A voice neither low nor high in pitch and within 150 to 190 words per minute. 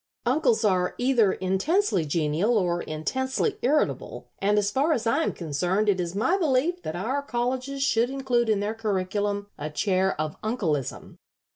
No: high, 215 Hz; average, 160 wpm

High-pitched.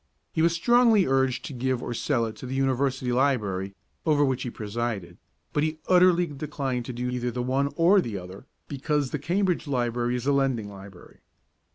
No: low, 130 Hz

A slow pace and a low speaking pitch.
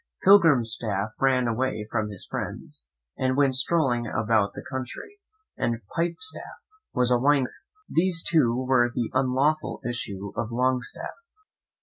Yes: slow, 130 wpm; low, 125 Hz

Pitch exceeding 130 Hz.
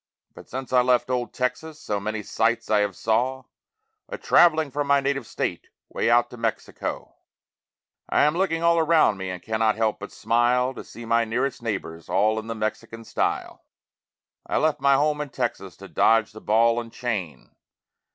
No: low, 120 Hz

